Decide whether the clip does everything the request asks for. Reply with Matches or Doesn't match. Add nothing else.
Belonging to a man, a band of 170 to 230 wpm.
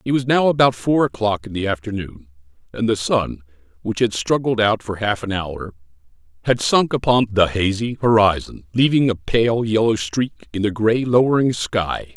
Matches